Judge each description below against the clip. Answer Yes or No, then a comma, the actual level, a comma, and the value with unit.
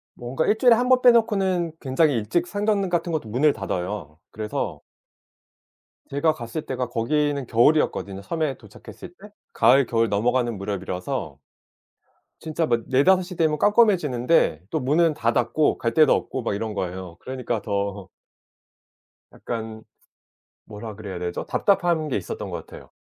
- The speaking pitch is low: Yes, low, 130 Hz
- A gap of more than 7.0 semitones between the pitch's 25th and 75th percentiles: Yes, wide, 7.5 semitones